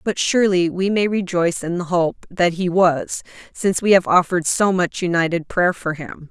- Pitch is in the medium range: Yes, medium, 180 Hz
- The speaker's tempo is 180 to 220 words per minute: Yes, average, 200 wpm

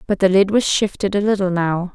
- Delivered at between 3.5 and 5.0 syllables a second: No, 5.5 syllables/s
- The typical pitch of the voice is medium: No, high, 195 Hz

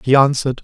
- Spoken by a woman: No, male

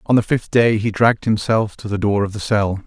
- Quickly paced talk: Yes, fast, 270 wpm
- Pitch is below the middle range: Yes, low, 105 Hz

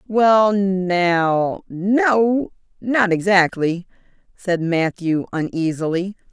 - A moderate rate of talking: No, slow, 55 wpm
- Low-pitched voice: No, high, 190 Hz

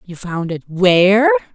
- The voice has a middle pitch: Yes, medium, 180 Hz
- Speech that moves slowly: Yes, slow, 115 wpm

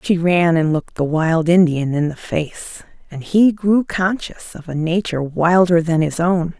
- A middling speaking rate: Yes, average, 190 wpm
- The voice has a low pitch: No, medium, 170 Hz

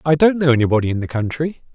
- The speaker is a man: Yes, male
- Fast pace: Yes, fast, 240 wpm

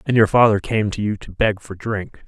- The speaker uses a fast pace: Yes, fast, 265 wpm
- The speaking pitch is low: Yes, low, 105 Hz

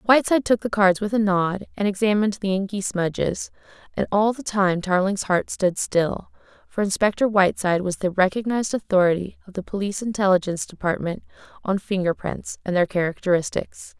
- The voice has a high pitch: Yes, high, 195 Hz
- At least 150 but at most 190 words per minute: Yes, average, 165 wpm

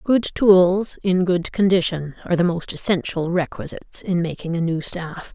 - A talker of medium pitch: Yes, medium, 180 Hz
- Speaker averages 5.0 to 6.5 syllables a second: No, 4.7 syllables/s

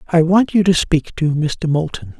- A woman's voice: No, male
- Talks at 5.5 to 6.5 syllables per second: No, 4.4 syllables/s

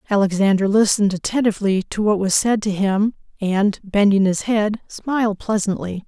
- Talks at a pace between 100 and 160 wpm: Yes, average, 150 wpm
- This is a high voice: Yes, high, 205 Hz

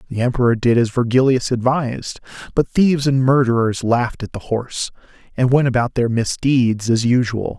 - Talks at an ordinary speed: Yes, average, 165 wpm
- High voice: No, low, 125 Hz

